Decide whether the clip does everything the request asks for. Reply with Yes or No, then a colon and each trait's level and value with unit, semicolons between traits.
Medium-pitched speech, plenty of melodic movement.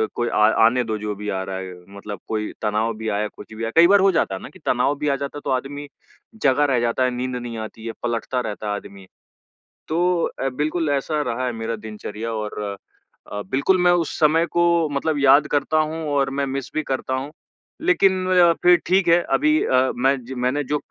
No: low, 130 Hz; wide, 5.7 semitones